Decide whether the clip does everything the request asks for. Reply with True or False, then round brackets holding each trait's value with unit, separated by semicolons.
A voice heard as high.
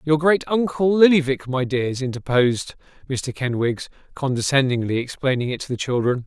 False (135 Hz)